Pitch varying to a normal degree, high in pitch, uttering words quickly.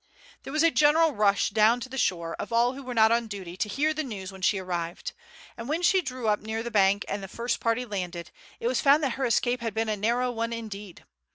Yes: average, 3.9 semitones; high, 230 Hz; fast, 255 wpm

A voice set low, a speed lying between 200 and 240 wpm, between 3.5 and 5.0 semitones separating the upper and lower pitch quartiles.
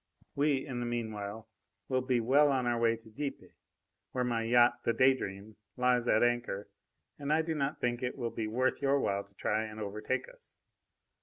No: low, 120 Hz; fast, 205 wpm; average, 2.9 semitones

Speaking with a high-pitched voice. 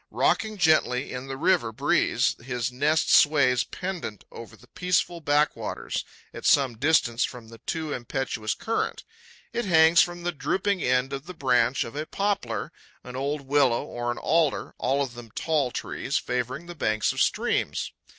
No: medium, 140 Hz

